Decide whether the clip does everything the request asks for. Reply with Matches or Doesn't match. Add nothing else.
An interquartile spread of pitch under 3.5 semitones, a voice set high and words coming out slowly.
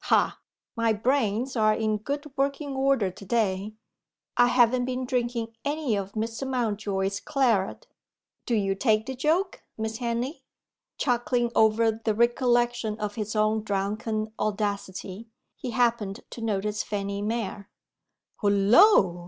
Matches